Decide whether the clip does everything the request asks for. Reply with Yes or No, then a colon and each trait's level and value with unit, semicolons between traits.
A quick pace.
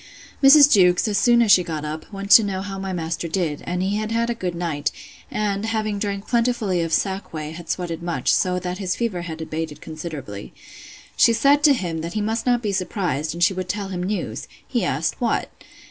Yes: fast, 220 wpm